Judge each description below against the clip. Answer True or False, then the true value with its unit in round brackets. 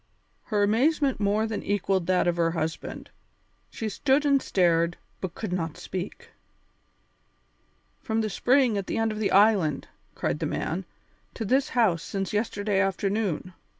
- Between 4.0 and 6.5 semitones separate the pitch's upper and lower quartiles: False (3.5 semitones)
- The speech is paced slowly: False (150 wpm)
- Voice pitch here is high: True (205 Hz)